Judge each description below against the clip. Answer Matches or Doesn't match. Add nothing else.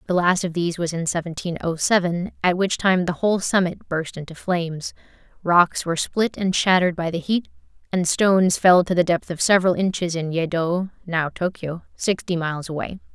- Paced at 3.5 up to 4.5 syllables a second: Doesn't match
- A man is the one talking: Doesn't match